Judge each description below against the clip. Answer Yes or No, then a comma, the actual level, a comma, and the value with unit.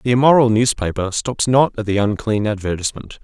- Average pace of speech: Yes, average, 165 wpm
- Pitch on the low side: Yes, low, 110 Hz